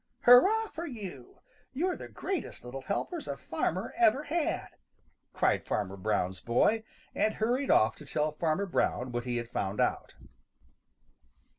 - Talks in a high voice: No, medium, 180 Hz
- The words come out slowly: No, average, 145 wpm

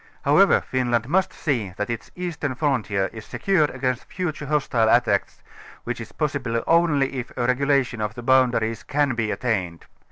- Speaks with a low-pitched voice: Yes, low, 125 Hz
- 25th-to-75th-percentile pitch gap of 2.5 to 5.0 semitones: Yes, average, 4.2 semitones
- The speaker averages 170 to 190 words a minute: No, average, 160 wpm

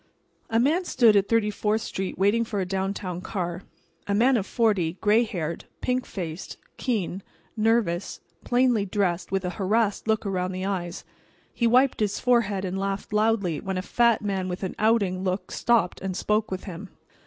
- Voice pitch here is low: No, high, 200 Hz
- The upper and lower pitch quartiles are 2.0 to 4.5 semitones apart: Yes, average, 3.4 semitones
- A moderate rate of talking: Yes, average, 175 wpm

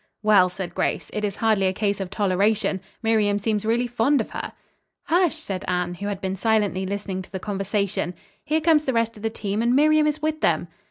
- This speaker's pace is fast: Yes, fast, 215 wpm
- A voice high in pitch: Yes, high, 210 Hz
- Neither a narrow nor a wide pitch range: Yes, average, 3.4 semitones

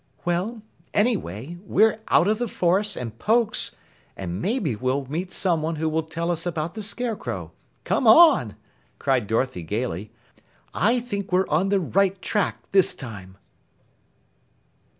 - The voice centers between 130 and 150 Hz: No, medium, 175 Hz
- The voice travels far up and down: Yes, wide, 8.0 semitones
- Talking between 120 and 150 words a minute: Yes, average, 140 wpm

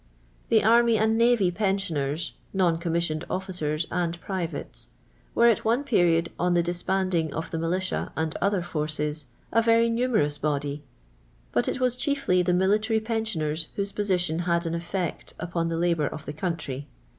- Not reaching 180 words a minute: Yes, average, 160 wpm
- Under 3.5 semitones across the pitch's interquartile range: No, average, 4.4 semitones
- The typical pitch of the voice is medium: Yes, medium, 175 Hz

